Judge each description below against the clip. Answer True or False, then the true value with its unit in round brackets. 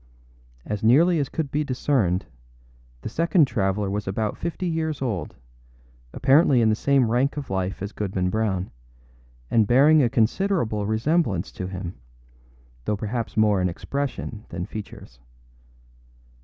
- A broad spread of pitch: True (6.2 semitones)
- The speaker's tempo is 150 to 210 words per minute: False (140 wpm)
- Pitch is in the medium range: False (110 Hz)